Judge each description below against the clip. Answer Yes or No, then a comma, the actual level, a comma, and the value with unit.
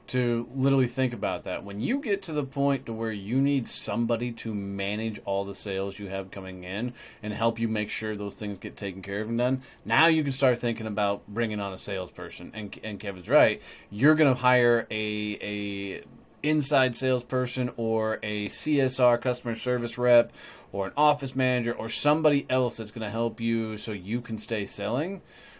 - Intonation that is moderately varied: Yes, average, 3.6 semitones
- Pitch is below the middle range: Yes, low, 115 Hz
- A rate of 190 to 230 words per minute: Yes, average, 195 wpm